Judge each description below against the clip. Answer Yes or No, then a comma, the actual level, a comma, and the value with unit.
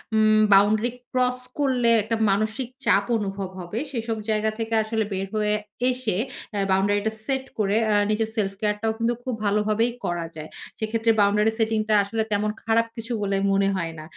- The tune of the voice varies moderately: No, narrow, 2.1 semitones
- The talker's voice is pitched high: Yes, high, 215 Hz